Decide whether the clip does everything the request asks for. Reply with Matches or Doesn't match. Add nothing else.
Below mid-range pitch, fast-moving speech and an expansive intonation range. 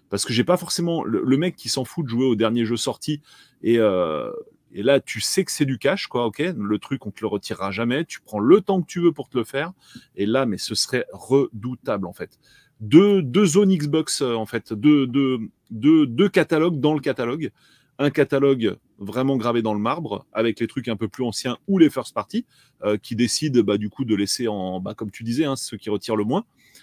Matches